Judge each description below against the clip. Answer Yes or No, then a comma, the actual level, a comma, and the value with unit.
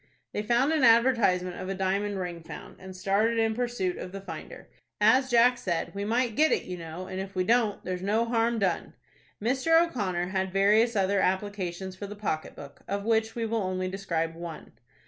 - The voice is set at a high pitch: Yes, high, 200 Hz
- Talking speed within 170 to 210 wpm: Yes, average, 200 wpm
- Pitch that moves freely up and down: No, average, 3.7 semitones